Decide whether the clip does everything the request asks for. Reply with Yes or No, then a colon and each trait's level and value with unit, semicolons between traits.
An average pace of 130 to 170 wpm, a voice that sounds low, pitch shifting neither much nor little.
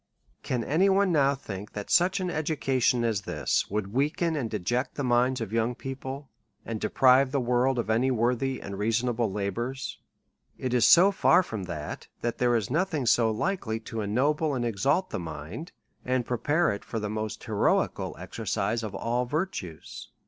No: average, 180 wpm; low, 125 Hz; average, 4.2 semitones